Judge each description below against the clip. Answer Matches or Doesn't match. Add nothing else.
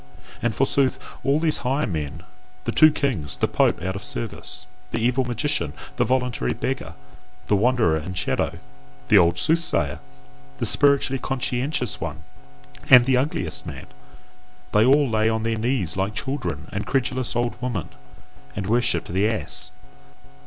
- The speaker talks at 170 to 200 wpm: Doesn't match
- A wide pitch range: Matches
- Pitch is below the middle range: Matches